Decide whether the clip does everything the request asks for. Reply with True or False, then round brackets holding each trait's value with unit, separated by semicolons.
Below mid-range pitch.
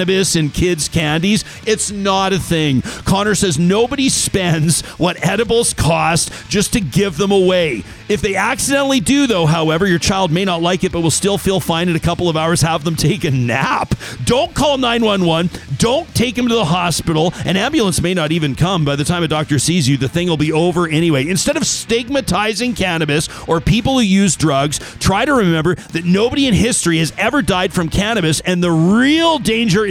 False (180 Hz)